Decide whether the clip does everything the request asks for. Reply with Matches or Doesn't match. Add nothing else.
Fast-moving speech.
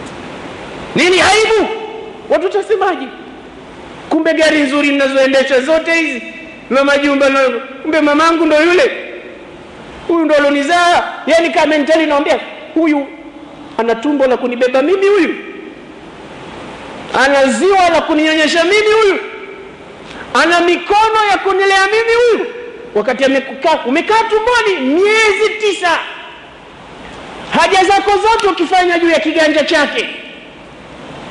Doesn't match